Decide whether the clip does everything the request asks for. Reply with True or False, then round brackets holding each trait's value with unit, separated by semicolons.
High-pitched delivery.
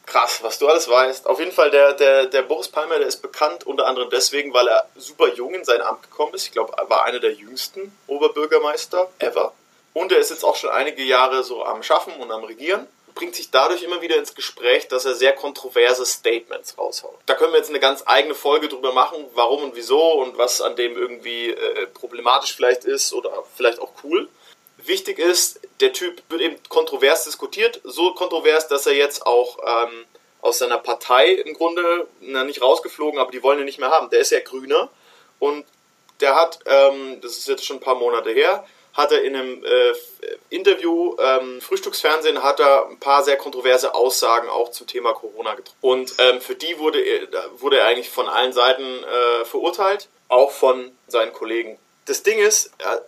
True (380 Hz)